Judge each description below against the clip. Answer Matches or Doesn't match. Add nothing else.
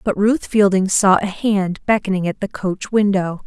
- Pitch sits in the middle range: Doesn't match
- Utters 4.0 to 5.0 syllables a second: Matches